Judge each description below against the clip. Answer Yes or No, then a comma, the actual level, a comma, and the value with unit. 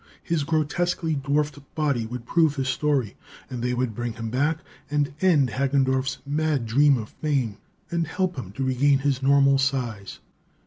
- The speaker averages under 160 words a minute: No, average, 165 wpm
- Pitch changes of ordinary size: Yes, average, 3.0 semitones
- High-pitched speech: No, medium, 140 Hz